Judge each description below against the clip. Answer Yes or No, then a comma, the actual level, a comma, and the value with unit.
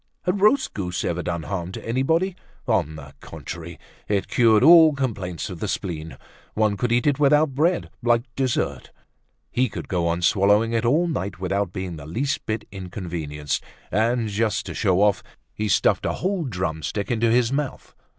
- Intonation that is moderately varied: No, wide, 6.4 semitones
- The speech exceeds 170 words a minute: Yes, average, 180 wpm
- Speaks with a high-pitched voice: No, low, 105 Hz